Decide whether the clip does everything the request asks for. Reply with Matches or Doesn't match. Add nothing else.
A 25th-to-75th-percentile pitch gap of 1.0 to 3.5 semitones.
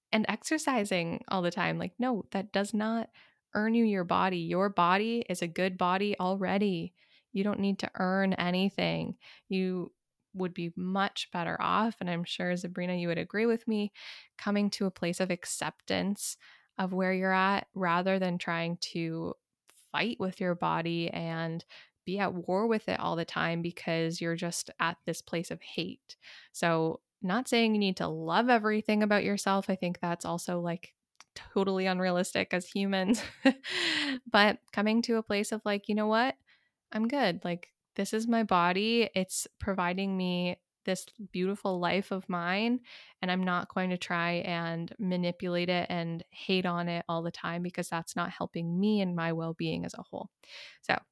Matches